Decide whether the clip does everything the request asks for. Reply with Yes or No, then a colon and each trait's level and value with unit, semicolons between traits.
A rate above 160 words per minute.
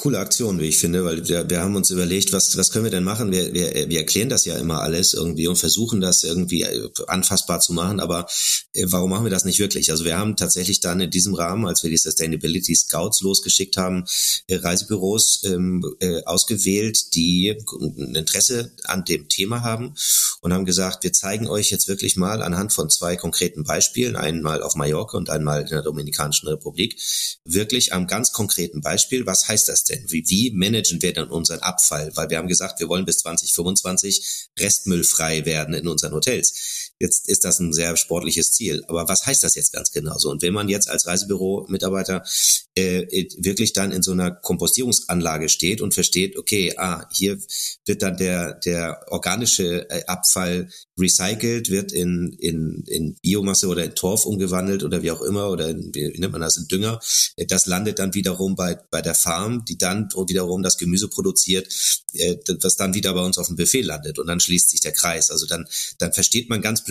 Yes: fast, 190 wpm